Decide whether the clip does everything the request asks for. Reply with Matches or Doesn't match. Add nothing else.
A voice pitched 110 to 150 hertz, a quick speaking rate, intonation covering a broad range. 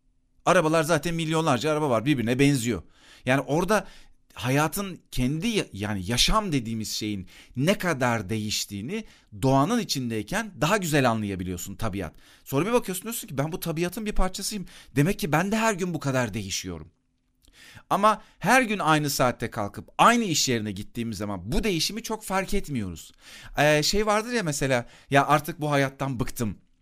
Matches